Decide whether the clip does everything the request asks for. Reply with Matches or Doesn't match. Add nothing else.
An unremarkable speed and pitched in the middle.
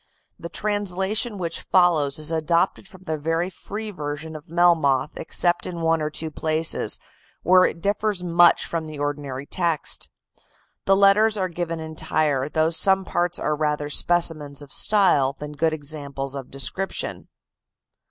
Matches